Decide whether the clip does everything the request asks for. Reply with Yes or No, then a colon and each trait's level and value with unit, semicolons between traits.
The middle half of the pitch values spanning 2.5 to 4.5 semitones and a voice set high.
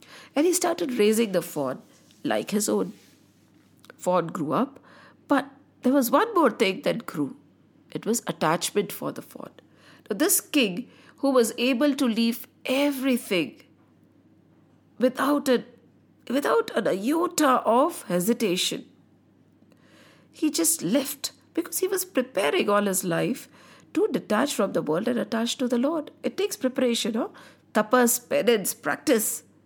Yes: average, 4.1 semitones; very high, 255 Hz